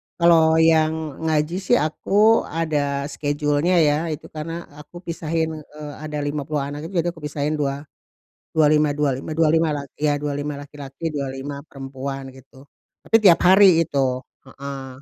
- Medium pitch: Yes, medium, 150 Hz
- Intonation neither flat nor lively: No, narrow, 2.3 semitones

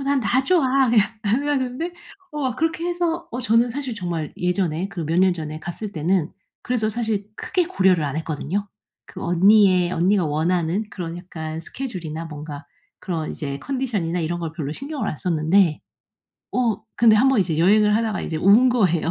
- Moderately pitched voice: No, high, 195 Hz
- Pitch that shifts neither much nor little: No, wide, 6.7 semitones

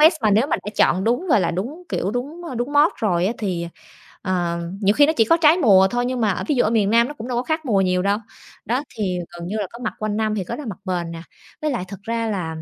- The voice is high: Yes, high, 215 Hz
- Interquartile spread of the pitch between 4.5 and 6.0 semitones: Yes, average, 5.2 semitones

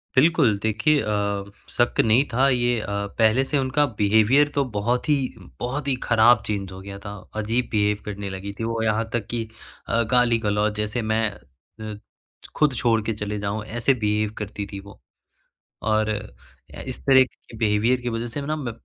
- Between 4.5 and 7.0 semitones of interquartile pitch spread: No, average, 2.9 semitones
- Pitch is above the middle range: No, low, 110 Hz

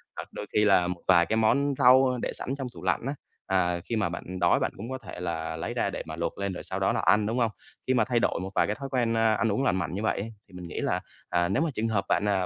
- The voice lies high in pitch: No, low, 105 Hz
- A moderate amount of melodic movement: Yes, average, 4.8 semitones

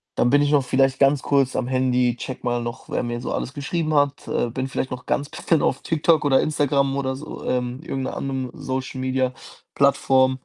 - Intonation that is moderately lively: No, narrow, 1.7 semitones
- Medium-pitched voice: No, low, 130 Hz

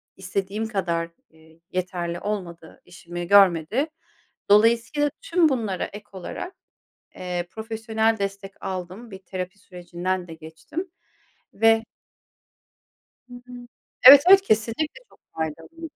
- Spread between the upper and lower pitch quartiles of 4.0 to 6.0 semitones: Yes, average, 4.3 semitones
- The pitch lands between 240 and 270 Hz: No, high, 195 Hz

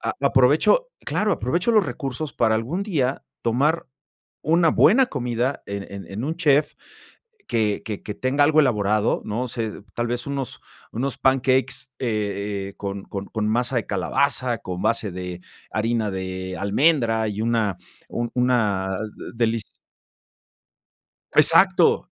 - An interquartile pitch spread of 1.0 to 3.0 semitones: No, average, 4.6 semitones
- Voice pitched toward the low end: Yes, low, 115 Hz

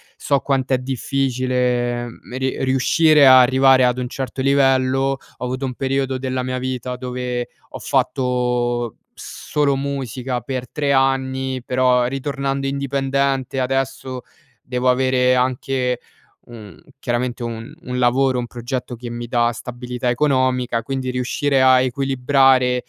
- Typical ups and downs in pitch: No, narrow, 1.3 semitones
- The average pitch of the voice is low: Yes, low, 130 Hz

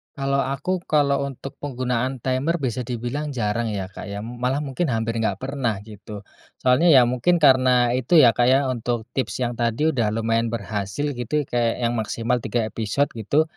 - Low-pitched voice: Yes, low, 125 Hz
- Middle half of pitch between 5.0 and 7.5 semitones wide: No, average, 3.2 semitones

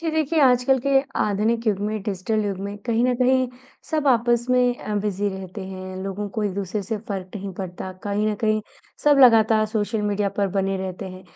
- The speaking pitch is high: Yes, high, 210 Hz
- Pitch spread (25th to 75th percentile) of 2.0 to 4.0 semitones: Yes, average, 3.3 semitones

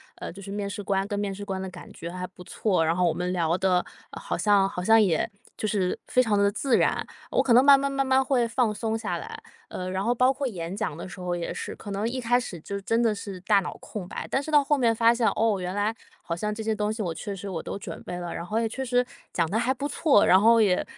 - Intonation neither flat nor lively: Yes, average, 4.2 semitones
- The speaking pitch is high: Yes, high, 205 Hz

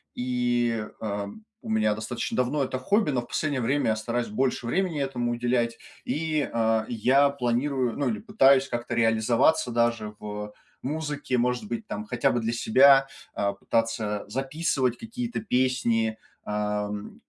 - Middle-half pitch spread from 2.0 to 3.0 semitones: No, average, 3.8 semitones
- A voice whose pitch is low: Yes, low, 120 Hz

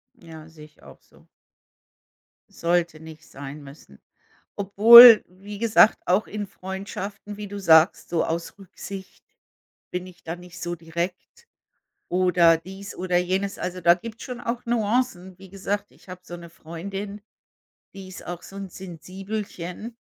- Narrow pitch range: No, average, 3.0 semitones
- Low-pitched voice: No, medium, 185 Hz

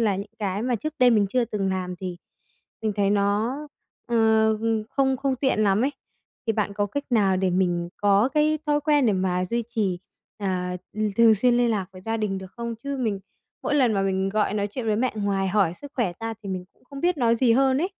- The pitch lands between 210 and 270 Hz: Yes, high, 215 Hz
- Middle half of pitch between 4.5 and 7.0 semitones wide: No, average, 4.1 semitones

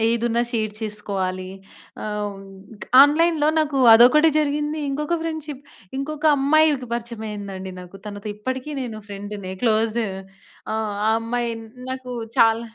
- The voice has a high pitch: Yes, high, 235 Hz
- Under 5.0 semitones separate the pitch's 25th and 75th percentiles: No, wide, 5.6 semitones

